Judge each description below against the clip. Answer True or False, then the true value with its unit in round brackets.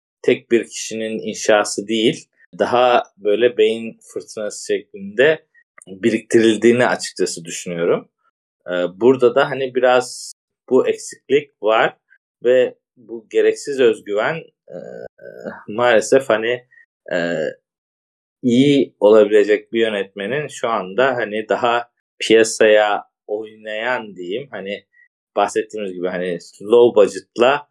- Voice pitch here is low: True (125 Hz)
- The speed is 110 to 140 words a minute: False (100 wpm)